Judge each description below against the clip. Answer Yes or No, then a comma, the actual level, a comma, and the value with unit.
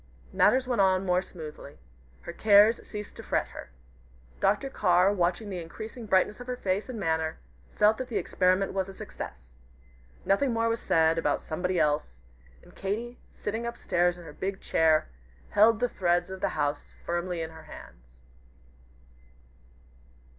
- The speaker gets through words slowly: No, average, 160 wpm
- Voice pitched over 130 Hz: Yes, high, 190 Hz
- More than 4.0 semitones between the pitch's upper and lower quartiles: Yes, average, 4.6 semitones